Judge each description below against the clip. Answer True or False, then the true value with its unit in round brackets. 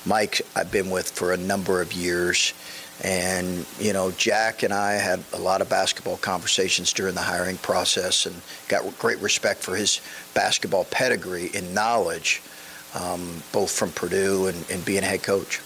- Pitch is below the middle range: True (90 Hz)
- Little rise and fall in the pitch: True (1.8 semitones)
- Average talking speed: True (170 wpm)